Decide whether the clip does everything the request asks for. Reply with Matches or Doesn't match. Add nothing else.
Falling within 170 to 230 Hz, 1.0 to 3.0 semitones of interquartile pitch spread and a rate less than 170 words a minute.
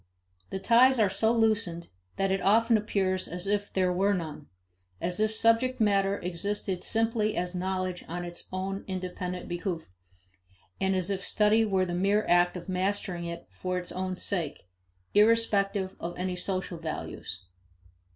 Matches